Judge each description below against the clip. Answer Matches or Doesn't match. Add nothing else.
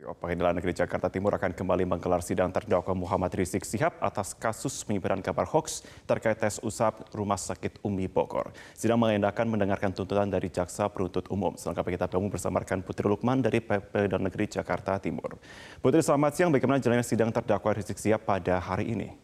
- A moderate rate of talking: Doesn't match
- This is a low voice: Matches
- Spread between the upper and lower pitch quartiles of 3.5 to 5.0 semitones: Doesn't match